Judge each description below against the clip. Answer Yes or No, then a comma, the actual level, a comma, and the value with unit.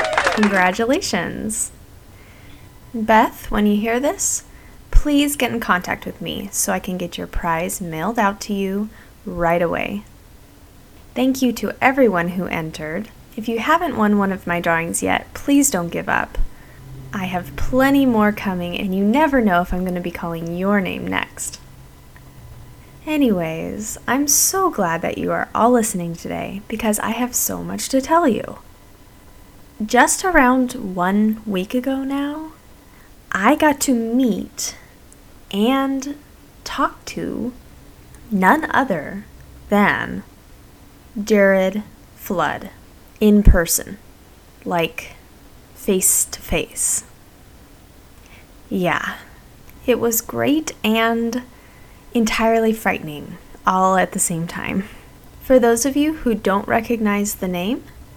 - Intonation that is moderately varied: No, wide, 6.0 semitones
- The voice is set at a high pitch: Yes, high, 210 Hz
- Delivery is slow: Yes, slow, 130 wpm